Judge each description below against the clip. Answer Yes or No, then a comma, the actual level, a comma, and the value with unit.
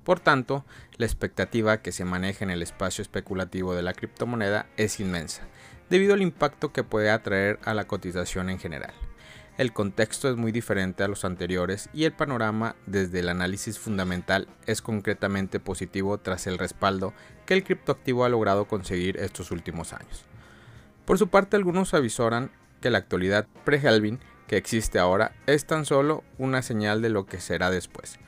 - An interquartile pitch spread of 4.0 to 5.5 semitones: Yes, average, 4.7 semitones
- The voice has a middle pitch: No, low, 105 Hz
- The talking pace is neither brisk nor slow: Yes, average, 170 wpm